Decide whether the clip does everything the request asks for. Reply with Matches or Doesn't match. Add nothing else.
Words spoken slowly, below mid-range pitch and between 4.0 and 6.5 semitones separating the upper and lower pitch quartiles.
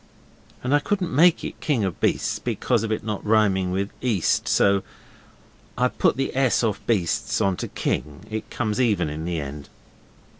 Doesn't match